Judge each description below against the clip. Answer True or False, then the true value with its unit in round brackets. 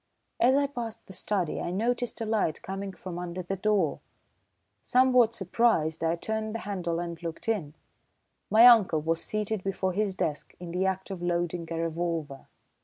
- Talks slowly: False (175 wpm)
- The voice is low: False (190 Hz)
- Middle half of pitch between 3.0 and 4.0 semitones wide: False (4.4 semitones)